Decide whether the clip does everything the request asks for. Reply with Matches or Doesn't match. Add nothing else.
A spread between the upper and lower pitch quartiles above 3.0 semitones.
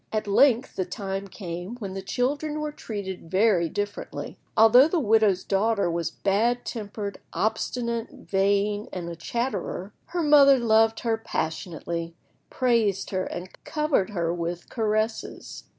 Matches